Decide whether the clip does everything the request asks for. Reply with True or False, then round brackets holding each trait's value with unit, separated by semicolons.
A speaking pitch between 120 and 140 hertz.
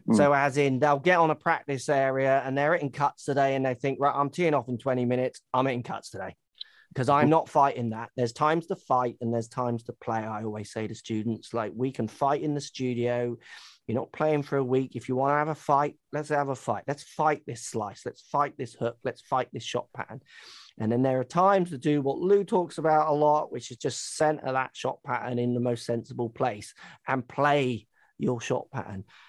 True (135 Hz)